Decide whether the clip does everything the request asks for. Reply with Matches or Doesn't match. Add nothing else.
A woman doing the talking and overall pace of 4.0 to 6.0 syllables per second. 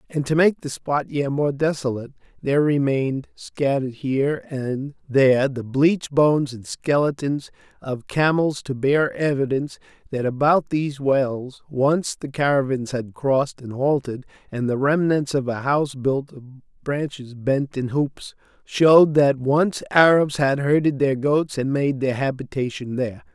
Doesn't match